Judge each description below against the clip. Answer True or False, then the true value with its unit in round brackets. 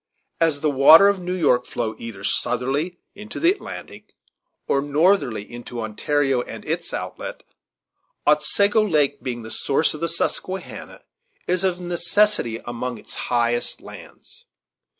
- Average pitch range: False (6.8 semitones)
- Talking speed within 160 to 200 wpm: False (135 wpm)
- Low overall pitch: False (145 Hz)